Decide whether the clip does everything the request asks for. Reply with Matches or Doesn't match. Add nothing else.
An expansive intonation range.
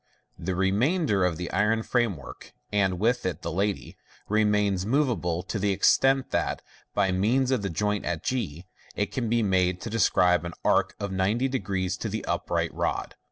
Doesn't match